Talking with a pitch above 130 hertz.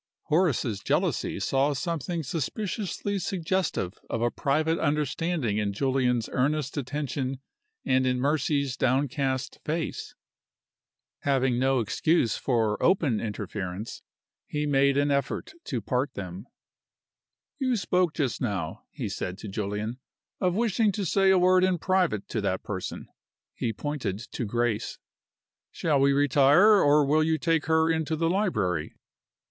Yes: medium, 140 Hz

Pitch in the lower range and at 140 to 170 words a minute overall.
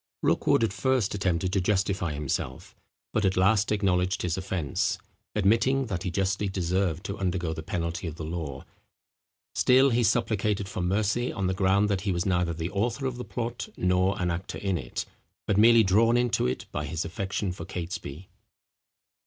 No: very low, 95 Hz; average, 180 wpm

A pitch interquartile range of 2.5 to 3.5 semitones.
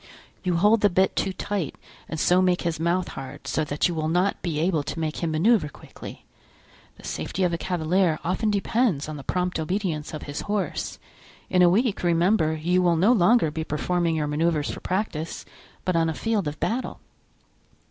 Yes: average, 3.2 semitones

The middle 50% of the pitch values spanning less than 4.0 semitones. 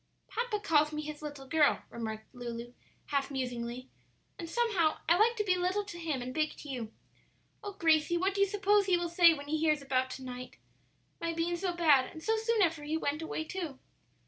No: average, 5.1 semitones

